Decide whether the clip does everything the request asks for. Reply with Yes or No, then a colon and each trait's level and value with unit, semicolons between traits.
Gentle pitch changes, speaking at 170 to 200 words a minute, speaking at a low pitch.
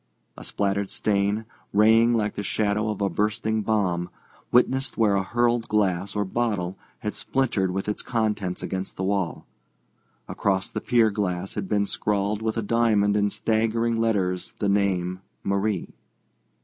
No: narrow, 2.3 semitones; average, 150 wpm; low, 105 Hz